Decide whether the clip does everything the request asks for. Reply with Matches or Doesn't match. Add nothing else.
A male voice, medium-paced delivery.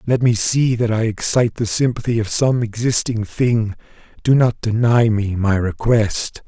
Matches